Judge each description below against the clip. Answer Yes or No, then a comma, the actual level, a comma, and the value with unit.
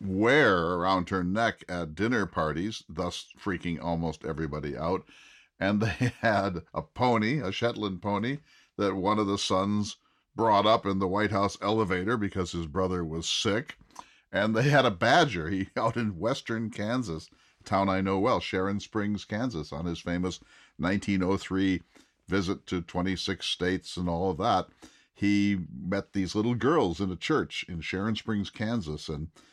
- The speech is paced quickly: No, average, 165 wpm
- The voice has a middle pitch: No, very low, 95 Hz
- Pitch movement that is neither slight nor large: Yes, average, 3.0 semitones